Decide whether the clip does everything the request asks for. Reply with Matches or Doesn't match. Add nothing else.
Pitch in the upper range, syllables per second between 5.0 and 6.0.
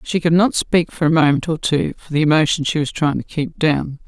Doesn't match